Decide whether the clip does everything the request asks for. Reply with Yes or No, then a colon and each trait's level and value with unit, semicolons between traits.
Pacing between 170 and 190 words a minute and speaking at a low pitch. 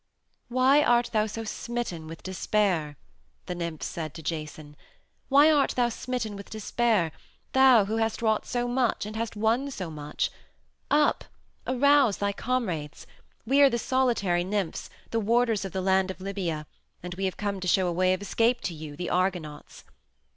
No: average, 175 wpm; high, 205 Hz